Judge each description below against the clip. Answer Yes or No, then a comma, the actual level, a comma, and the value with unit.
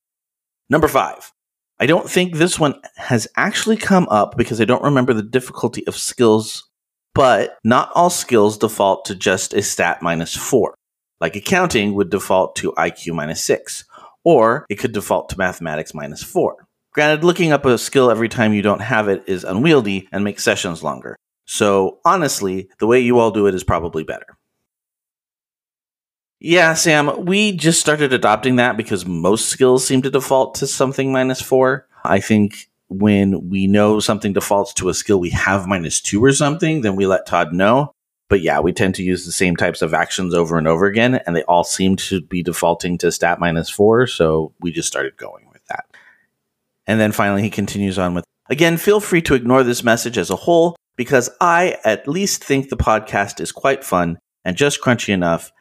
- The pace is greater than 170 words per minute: Yes, average, 190 wpm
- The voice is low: Yes, low, 110 Hz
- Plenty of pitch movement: Yes, wide, 6.1 semitones